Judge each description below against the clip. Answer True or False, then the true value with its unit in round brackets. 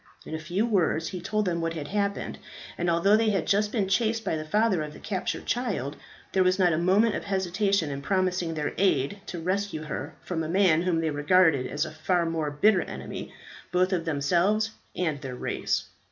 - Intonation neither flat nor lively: True (4.0 semitones)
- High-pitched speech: False (180 Hz)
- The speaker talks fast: True (210 wpm)